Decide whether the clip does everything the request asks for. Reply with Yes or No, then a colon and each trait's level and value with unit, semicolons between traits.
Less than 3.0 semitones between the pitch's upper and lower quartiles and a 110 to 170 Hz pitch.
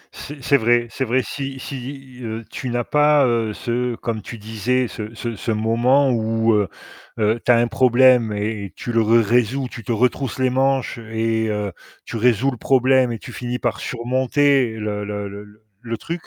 Yes: narrow, 2.6 semitones; low, 120 Hz